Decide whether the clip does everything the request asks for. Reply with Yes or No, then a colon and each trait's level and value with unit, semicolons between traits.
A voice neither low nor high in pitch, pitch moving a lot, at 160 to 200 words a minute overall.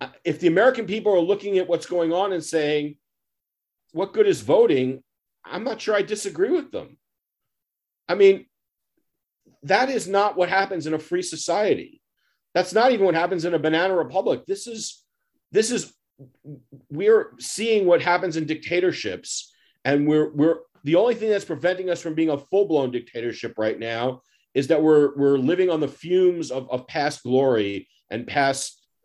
Yes: medium, 170 Hz; wide, 5.7 semitones; average, 170 wpm